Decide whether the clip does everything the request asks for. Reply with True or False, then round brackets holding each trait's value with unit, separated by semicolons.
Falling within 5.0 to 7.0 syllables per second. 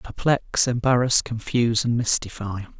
False (4.6 syllables/s)